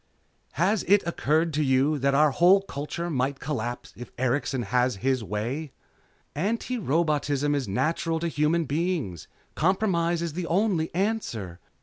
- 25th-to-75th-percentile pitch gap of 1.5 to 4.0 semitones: No, average, 4.5 semitones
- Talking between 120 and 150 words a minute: Yes, slow, 135 wpm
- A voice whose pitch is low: No, medium, 150 Hz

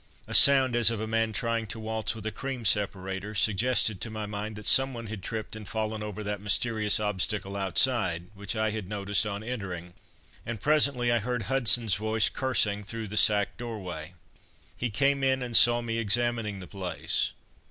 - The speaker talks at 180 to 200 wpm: Yes, average, 185 wpm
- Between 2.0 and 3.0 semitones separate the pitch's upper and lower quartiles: Yes, narrow, 2.6 semitones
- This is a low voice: Yes, low, 110 Hz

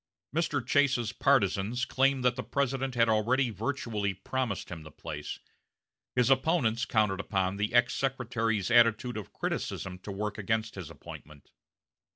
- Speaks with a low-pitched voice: Yes, low, 115 Hz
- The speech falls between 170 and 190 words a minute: No, average, 145 wpm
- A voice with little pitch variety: No, average, 4.3 semitones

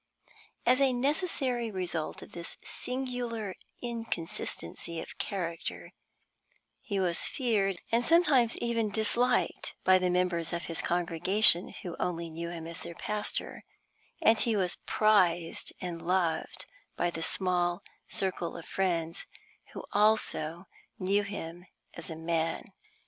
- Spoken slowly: Yes, slow, 125 wpm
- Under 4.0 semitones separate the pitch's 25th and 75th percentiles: No, average, 4.6 semitones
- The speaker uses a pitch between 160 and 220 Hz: Yes, medium, 185 Hz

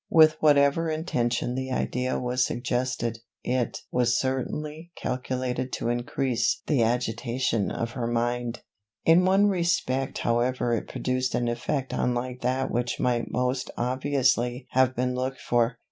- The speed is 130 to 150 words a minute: Yes, slow, 135 wpm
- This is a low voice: Yes, low, 125 Hz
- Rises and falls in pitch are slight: Yes, narrow, 1.7 semitones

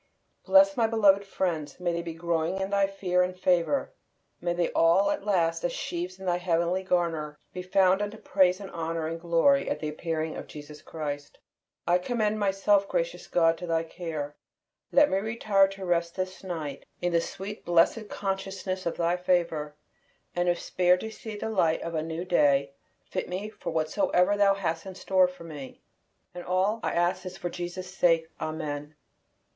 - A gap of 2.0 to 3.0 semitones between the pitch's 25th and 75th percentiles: Yes, average, 2.7 semitones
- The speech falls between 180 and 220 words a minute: Yes, average, 185 wpm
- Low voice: No, medium, 180 Hz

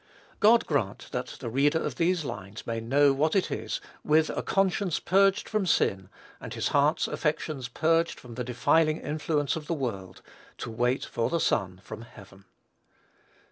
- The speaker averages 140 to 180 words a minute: Yes, average, 170 wpm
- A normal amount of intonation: No, wide, 6.1 semitones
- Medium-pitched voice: Yes, medium, 145 Hz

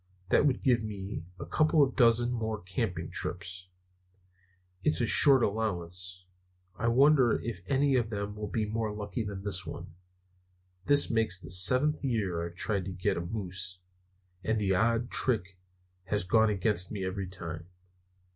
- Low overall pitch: Yes, low, 105 Hz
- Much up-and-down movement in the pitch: No, average, 4.2 semitones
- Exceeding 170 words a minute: No, average, 160 wpm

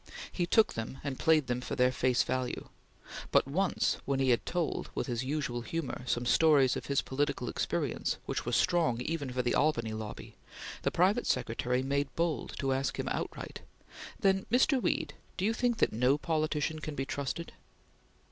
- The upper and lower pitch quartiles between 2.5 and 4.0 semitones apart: No, average, 4.6 semitones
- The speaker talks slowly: No, average, 180 wpm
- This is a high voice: No, medium, 140 Hz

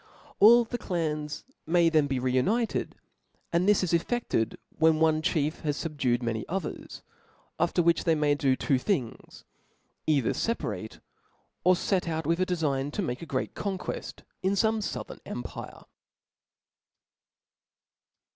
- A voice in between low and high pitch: Yes, medium, 160 Hz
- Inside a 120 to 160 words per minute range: Yes, average, 155 wpm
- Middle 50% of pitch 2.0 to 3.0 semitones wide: No, average, 4.6 semitones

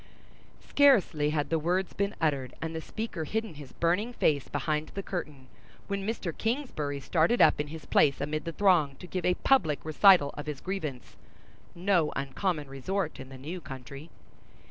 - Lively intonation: No, average, 5.0 semitones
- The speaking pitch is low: No, medium, 160 Hz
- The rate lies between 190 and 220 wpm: No, average, 165 wpm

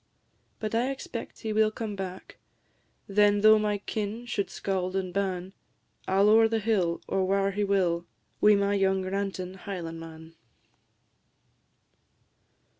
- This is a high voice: Yes, high, 200 Hz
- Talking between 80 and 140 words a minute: Yes, slow, 135 wpm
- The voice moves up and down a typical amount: No, narrow, 2.3 semitones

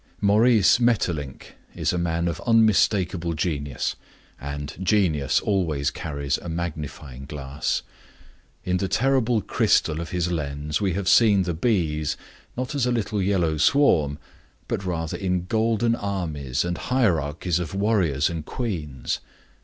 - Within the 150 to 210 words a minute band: No, slow, 135 wpm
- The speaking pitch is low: Yes, very low, 85 Hz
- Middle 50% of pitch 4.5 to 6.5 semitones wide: Yes, average, 5.3 semitones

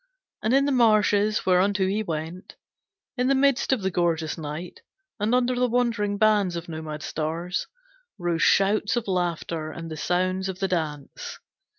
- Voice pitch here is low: No, high, 190 Hz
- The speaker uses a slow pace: No, average, 165 wpm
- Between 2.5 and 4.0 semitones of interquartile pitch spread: No, average, 4.4 semitones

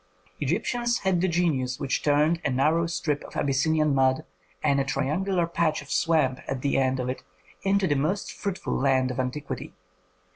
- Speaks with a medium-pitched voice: Yes, medium, 150 Hz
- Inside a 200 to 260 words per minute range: No, average, 175 wpm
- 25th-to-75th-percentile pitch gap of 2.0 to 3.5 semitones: No, average, 4.3 semitones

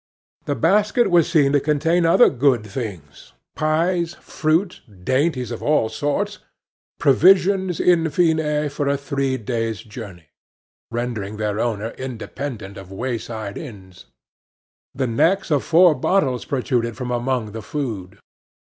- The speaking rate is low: Yes, slow, 130 wpm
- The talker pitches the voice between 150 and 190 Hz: No, low, 135 Hz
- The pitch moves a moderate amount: No, wide, 6.2 semitones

